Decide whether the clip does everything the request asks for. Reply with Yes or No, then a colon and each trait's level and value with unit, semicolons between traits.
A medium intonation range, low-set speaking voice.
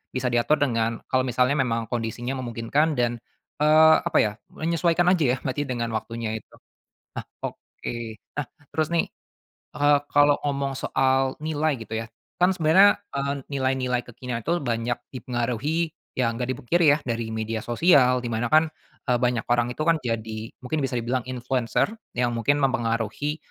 Yes: average, 3.8 semitones; low, 130 Hz